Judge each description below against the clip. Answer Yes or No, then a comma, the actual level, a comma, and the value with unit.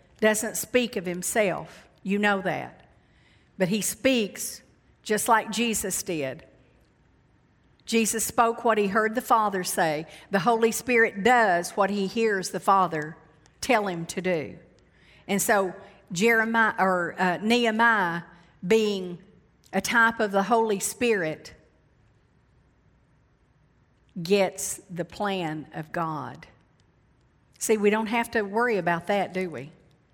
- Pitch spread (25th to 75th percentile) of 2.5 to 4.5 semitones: Yes, average, 3.9 semitones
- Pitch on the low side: No, high, 200 Hz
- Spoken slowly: Yes, slow, 125 wpm